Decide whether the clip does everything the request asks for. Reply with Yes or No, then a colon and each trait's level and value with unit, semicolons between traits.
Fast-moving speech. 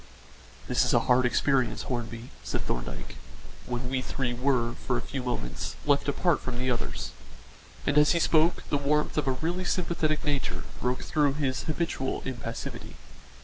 No: average, 165 wpm